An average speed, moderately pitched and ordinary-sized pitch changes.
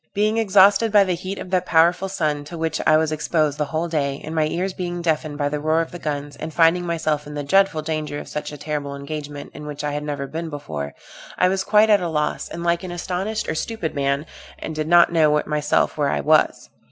No: fast, 240 wpm; medium, 155 Hz; average, 3.1 semitones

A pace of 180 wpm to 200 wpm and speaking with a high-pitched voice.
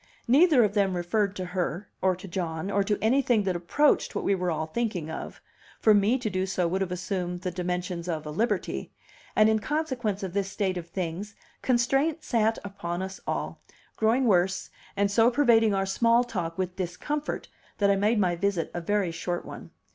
Yes: average, 195 wpm; high, 195 Hz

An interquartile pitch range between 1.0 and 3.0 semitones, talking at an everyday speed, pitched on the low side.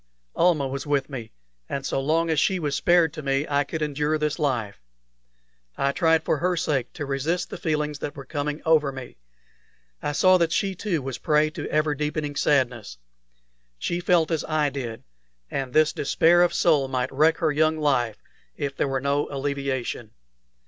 No: average, 2.7 semitones; average, 185 wpm; medium, 150 Hz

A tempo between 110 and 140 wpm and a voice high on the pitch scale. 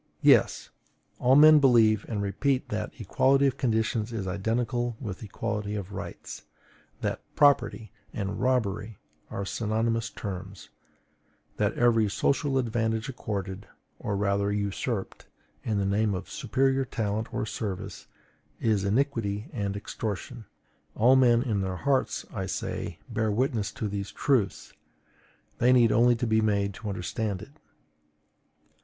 No: slow, 135 wpm; low, 110 Hz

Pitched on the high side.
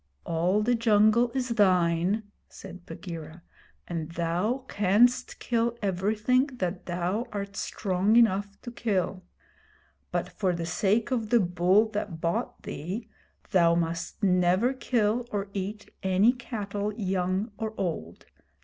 Yes: high, 200 Hz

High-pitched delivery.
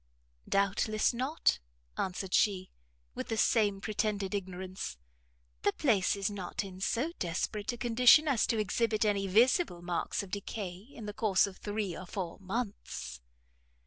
Yes: high, 205 Hz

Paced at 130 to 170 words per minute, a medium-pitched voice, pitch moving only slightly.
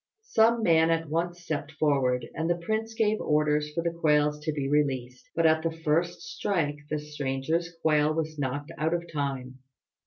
No: average, 180 wpm; medium, 155 Hz; narrow, 2.3 semitones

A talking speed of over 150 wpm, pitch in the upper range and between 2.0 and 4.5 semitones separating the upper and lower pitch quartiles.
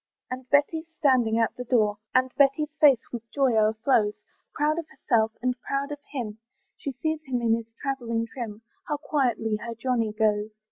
Yes: average, 175 wpm; high, 245 Hz; average, 3.7 semitones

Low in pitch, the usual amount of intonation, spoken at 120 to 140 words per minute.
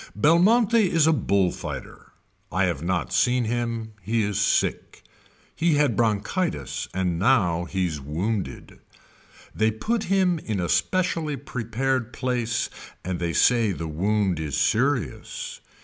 No: low, 110 Hz; wide, 7.6 semitones; slow, 135 wpm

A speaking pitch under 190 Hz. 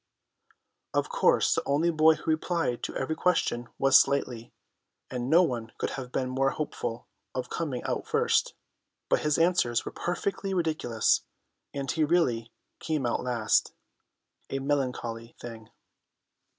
Yes: low, 135 Hz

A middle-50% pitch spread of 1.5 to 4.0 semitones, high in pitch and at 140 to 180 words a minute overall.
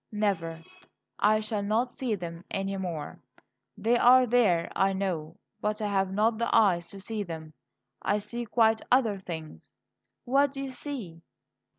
No: average, 4.7 semitones; high, 205 Hz; average, 160 wpm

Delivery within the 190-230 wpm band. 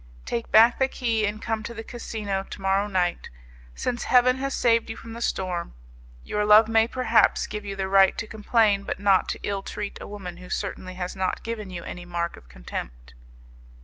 Yes: fast, 205 wpm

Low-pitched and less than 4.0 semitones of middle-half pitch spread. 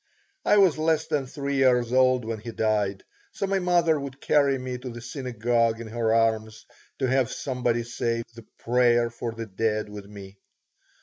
Yes: low, 120 Hz; average, 3.0 semitones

